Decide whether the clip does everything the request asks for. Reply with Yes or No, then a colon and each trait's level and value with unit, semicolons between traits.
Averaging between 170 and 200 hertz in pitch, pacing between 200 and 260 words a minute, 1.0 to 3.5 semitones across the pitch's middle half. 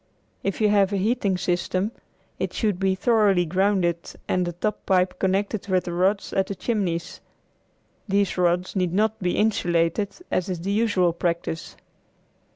No: high, 190 Hz; average, 160 wpm; narrow, 2.5 semitones